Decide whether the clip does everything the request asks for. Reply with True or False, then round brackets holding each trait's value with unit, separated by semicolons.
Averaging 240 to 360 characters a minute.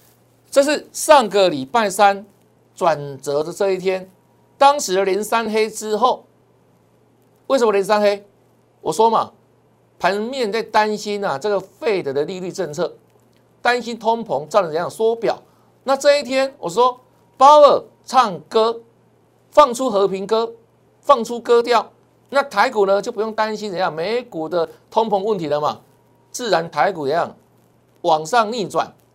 False (215 characters per minute)